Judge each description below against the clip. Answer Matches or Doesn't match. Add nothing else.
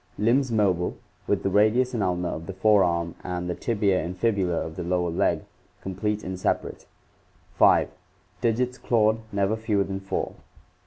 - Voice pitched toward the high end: Doesn't match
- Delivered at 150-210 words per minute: Matches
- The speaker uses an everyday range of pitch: Matches